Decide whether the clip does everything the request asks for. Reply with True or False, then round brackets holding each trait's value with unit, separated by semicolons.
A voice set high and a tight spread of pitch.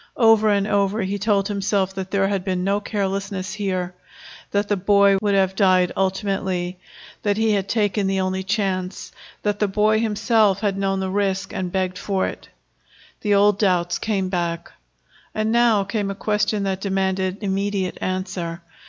True (195 Hz; 1.5 semitones)